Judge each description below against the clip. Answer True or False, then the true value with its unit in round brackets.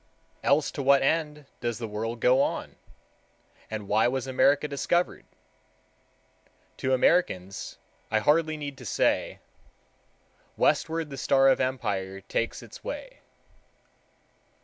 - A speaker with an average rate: False (120 wpm)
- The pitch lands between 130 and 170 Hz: True (135 Hz)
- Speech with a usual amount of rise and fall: True (4.8 semitones)